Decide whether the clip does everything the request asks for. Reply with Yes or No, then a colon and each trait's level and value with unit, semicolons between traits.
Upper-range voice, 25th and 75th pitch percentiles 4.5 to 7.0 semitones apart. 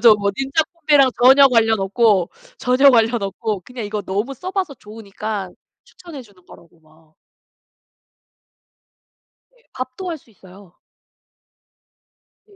Yes: high, 225 Hz; average, 5.3 semitones